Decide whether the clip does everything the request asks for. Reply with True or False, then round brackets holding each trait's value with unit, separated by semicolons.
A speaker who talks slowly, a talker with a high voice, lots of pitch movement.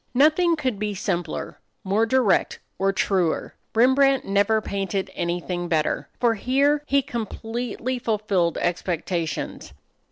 True (115 wpm; 210 Hz; 5.9 semitones)